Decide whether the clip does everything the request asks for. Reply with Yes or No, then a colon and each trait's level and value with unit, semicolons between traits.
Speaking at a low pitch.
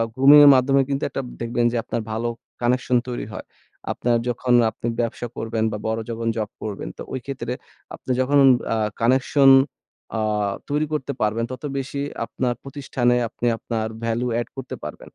Yes: low, 125 Hz